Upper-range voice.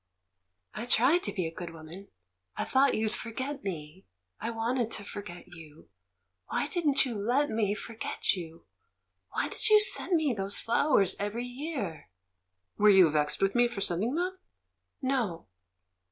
Yes: high, 215 Hz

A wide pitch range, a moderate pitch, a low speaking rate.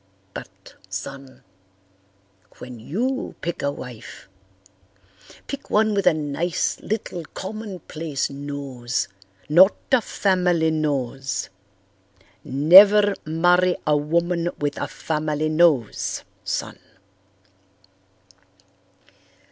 No: average, 4.5 semitones; medium, 155 Hz; slow, 85 wpm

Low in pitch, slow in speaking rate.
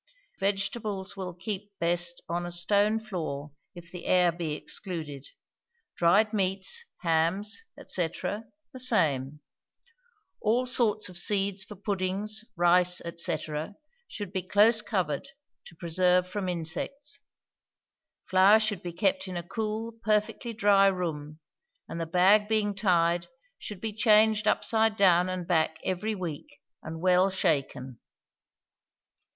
No: medium, 185 Hz; slow, 125 wpm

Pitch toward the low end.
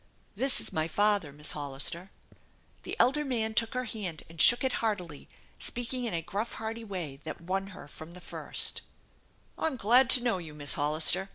No: high, 195 Hz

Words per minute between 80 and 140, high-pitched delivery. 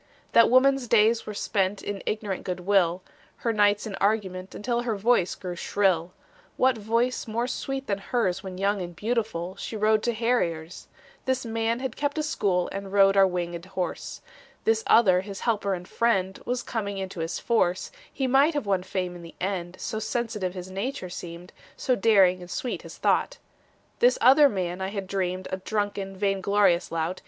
No: average, 185 wpm; high, 200 Hz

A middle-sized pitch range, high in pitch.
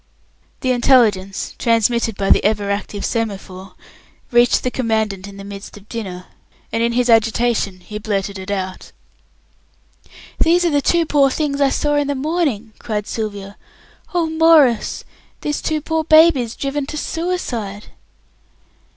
No: wide, 6.1 semitones; high, 230 Hz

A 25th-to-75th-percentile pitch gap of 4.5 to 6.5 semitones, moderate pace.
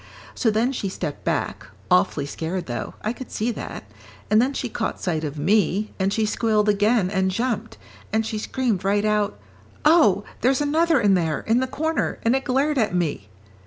Yes: average, 4.8 semitones; average, 190 wpm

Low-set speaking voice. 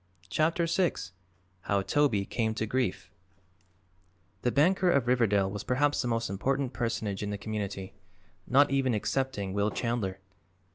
Yes: low, 115 Hz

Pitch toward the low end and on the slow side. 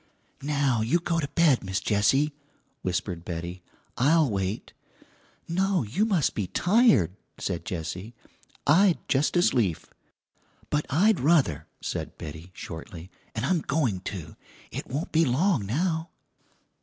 Yes: low, 130 Hz; slow, 130 wpm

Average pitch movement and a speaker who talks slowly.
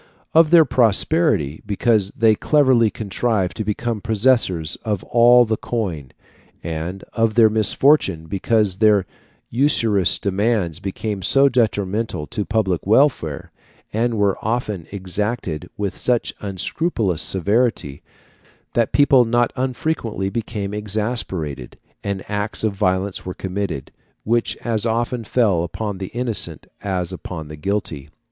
Yes: average, 3.9 semitones; slow, 125 wpm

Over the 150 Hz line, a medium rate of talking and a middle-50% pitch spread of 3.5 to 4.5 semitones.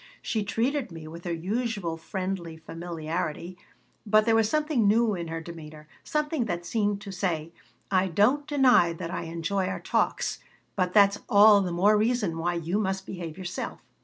Yes: high, 190 Hz; average, 170 wpm; average, 4.2 semitones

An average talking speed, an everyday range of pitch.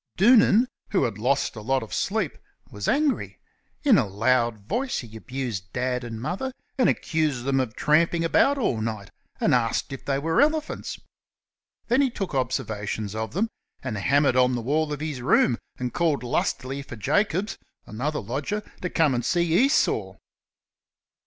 No: average, 165 wpm; wide, 6.6 semitones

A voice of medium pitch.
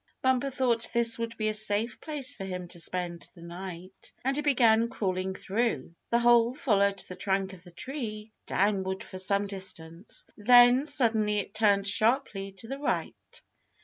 No: high, 210 Hz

